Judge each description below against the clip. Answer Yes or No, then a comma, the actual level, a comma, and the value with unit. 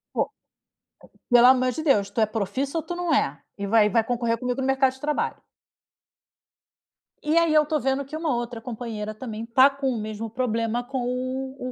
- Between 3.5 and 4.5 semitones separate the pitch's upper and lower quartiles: No, average, 3.0 semitones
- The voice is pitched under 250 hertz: No, very high, 255 Hz